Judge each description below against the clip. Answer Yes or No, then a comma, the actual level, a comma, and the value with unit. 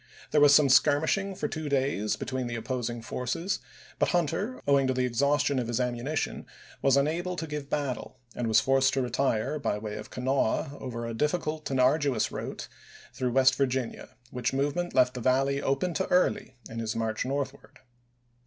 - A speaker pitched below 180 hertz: Yes, low, 135 Hz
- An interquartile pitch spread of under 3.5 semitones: Yes, average, 2.8 semitones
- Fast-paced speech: No, average, 180 wpm